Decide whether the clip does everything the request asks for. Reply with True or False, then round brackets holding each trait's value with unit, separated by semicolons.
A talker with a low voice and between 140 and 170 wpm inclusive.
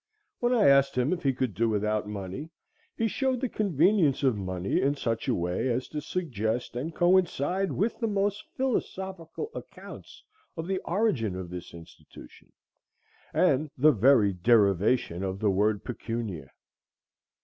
True (130 Hz; 150 wpm)